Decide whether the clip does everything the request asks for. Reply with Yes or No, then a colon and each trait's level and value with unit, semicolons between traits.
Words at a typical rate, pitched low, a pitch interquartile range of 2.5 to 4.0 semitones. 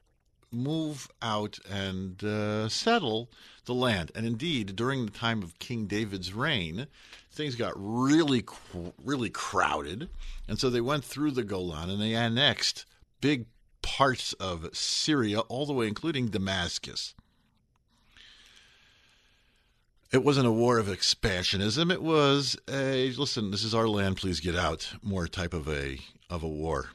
No: average, 145 wpm; low, 115 Hz; average, 5.1 semitones